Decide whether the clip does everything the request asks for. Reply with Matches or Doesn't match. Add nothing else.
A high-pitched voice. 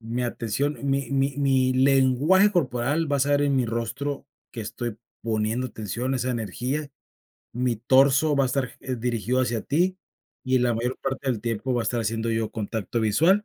Doesn't match